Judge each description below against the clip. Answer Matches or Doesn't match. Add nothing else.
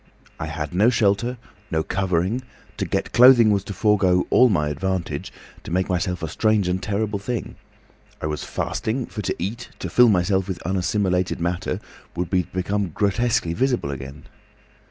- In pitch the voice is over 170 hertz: Doesn't match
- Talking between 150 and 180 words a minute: Matches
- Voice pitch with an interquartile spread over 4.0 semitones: Doesn't match